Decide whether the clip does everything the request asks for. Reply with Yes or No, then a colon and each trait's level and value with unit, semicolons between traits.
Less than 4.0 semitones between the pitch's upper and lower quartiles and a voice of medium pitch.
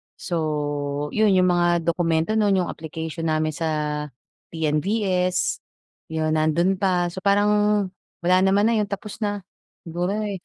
Yes: average, 3.6 semitones; medium, 180 Hz